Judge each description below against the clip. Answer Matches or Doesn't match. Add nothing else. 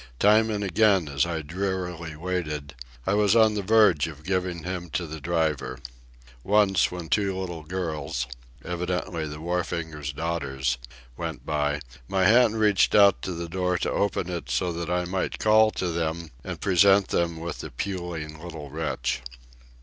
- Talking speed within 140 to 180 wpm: Matches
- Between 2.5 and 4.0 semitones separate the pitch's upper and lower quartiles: Matches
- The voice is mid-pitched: Doesn't match